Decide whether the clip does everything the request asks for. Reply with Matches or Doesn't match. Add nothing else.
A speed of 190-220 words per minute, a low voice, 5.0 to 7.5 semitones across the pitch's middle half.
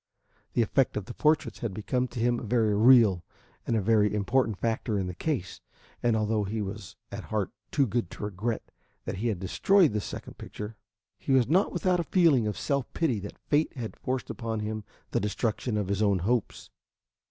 Doesn't match